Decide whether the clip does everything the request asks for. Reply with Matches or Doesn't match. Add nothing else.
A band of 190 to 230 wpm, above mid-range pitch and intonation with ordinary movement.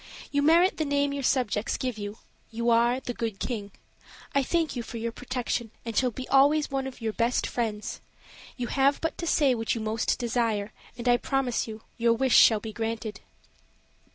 Matches